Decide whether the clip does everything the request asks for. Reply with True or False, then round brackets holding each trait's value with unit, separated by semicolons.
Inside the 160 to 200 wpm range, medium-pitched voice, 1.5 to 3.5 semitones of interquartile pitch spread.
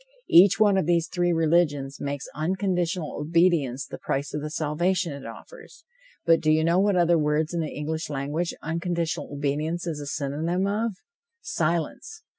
True (165 wpm; 165 Hz; 2.9 semitones)